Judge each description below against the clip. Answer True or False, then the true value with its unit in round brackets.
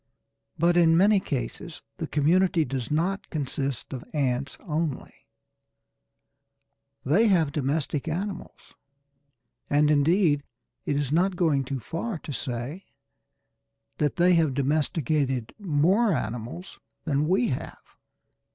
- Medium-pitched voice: True (155 Hz)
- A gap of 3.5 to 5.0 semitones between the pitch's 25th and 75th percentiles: True (4.0 semitones)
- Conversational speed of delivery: False (115 wpm)